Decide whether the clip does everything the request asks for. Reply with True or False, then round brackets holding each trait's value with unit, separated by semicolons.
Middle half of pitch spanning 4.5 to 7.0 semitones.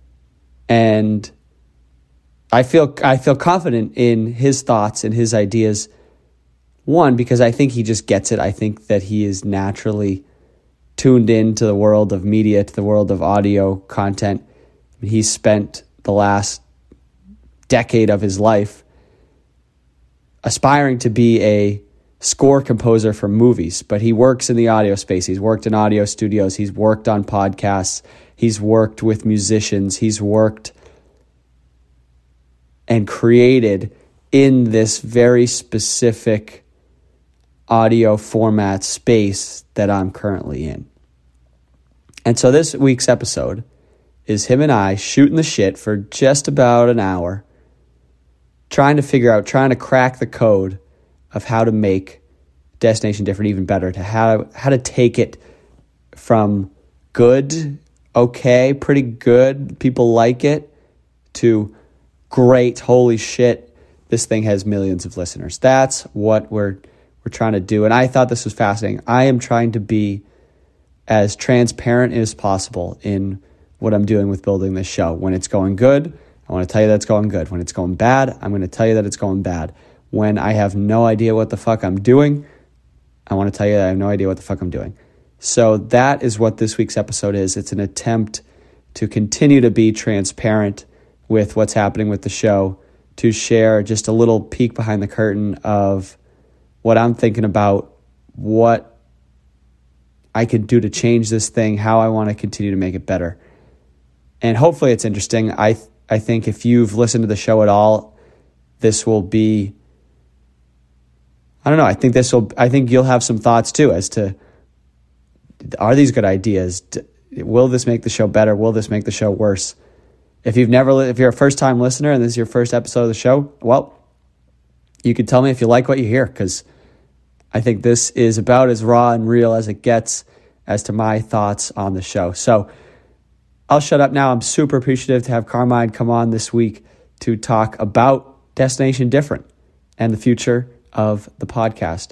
False (3.9 semitones)